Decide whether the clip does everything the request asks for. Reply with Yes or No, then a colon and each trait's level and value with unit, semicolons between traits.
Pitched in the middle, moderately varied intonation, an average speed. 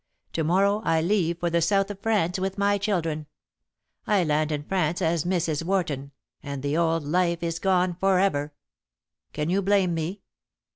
Yes: medium, 170 Hz; average, 3.3 semitones; average, 175 wpm